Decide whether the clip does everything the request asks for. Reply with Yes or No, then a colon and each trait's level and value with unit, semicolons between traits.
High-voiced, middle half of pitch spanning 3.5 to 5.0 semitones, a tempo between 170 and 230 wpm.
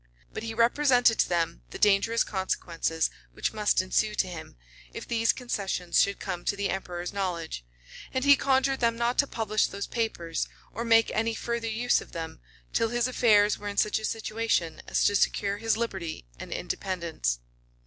Yes: high, 210 Hz; average, 4.7 semitones; average, 180 wpm